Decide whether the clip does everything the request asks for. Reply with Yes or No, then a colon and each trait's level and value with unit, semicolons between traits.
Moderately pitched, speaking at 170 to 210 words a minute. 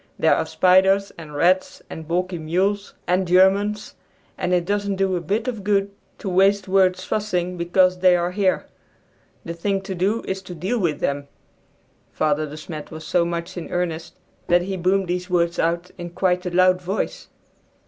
Yes: medium, 180 Hz; average, 180 wpm